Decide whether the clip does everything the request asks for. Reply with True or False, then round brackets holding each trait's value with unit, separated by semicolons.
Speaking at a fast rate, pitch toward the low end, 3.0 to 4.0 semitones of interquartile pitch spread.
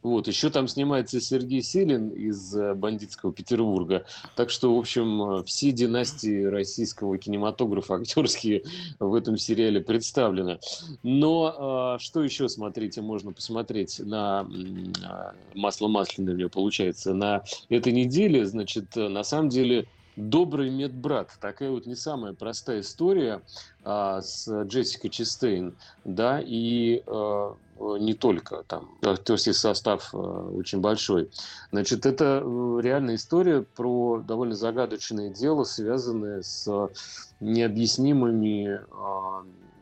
False (115 wpm; 110 Hz; 3.5 semitones)